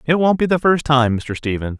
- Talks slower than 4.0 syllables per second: No, 5.3 syllables/s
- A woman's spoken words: No, male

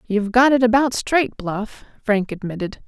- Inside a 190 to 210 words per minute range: No, average, 165 wpm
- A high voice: Yes, high, 225 Hz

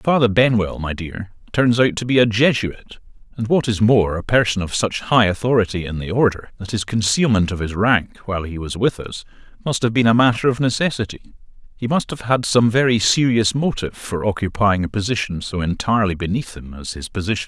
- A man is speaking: Yes, male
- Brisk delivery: Yes, fast, 215 wpm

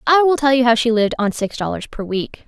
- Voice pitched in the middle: No, high, 245 Hz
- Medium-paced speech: No, fast, 290 wpm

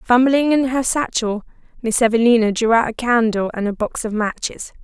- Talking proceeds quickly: No, average, 185 wpm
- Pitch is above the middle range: Yes, high, 235 Hz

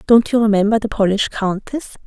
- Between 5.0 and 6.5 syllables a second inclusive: Yes, 5.7 syllables/s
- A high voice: Yes, high, 215 Hz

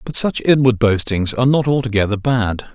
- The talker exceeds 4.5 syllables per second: Yes, 5.4 syllables/s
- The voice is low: Yes, low, 120 Hz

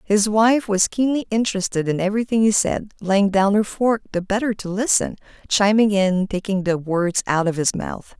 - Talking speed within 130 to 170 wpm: No, average, 190 wpm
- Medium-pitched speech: No, high, 205 Hz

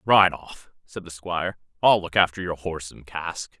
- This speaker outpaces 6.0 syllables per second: No, 4.8 syllables/s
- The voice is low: Yes, very low, 85 Hz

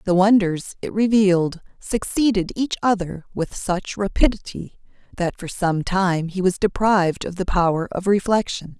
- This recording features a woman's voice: Yes, female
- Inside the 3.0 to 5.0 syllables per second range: Yes, 4.6 syllables/s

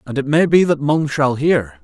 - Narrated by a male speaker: Yes, male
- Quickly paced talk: Yes, fast, 260 wpm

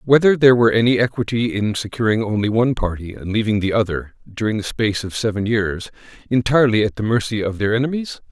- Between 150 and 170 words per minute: No, average, 195 wpm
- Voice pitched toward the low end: Yes, low, 110 Hz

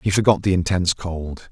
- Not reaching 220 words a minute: Yes, average, 200 wpm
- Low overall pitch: Yes, very low, 90 Hz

